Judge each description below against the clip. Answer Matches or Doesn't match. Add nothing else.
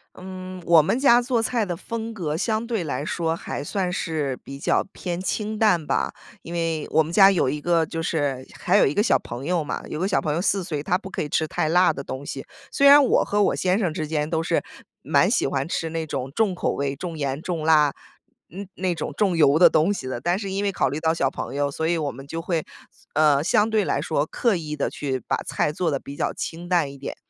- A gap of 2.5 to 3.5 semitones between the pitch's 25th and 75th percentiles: Doesn't match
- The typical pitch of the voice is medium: Matches